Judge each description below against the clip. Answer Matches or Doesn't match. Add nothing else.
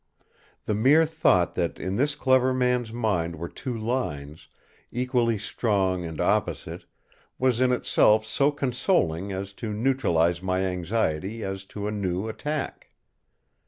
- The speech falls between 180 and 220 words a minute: Doesn't match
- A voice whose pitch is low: Matches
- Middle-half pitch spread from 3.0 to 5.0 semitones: Doesn't match